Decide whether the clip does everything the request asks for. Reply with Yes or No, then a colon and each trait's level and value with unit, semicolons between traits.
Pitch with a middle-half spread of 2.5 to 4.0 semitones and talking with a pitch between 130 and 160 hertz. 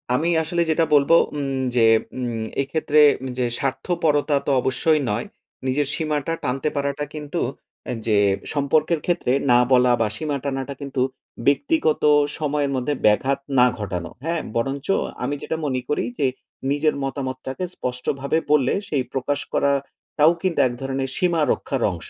Yes: average, 2.8 semitones; medium, 140 Hz